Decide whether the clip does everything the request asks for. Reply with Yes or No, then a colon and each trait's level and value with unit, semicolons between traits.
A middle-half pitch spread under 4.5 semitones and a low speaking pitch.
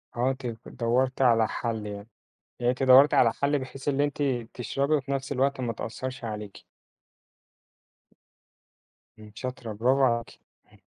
Yes: average, 2.8 semitones; low, 130 Hz